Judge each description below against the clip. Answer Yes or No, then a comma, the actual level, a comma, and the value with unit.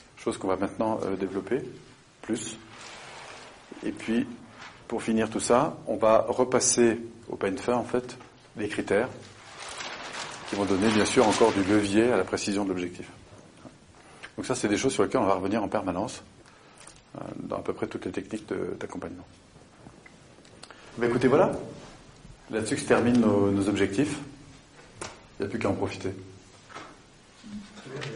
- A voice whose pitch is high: No, low, 110 Hz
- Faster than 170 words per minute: No, average, 160 wpm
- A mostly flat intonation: No, average, 3.8 semitones